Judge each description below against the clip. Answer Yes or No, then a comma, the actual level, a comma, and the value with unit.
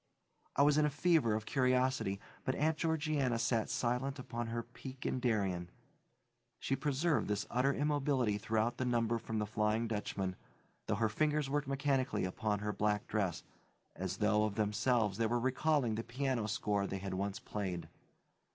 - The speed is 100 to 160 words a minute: No, average, 170 wpm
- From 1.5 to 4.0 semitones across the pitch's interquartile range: No, average, 4.4 semitones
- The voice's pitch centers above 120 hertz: No, low, 115 Hz